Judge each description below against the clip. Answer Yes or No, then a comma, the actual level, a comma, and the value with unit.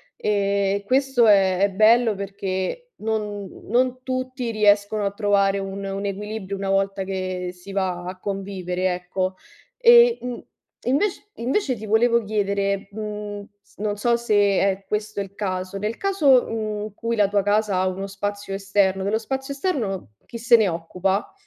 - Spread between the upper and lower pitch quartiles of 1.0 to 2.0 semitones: No, narrow, 2.6 semitones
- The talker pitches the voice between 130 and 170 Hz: No, high, 205 Hz